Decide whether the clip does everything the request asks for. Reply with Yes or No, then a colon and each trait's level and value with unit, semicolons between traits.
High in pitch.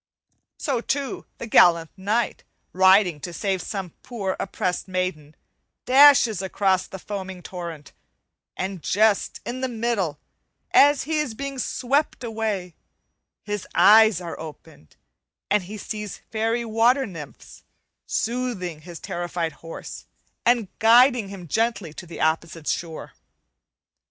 Yes: high, 200 Hz